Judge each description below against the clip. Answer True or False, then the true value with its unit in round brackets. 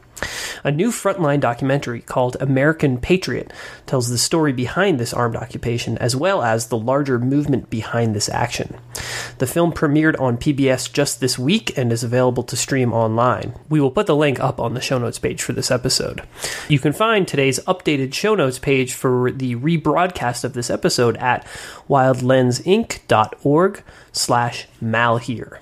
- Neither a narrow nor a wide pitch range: True (3.6 semitones)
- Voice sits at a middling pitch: False (130 Hz)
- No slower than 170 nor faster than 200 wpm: False (160 wpm)